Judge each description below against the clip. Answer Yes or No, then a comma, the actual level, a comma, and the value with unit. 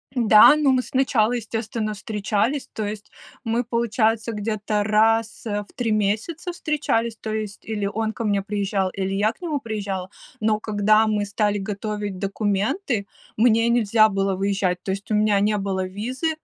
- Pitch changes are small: Yes, narrow, 2.0 semitones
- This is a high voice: Yes, high, 215 Hz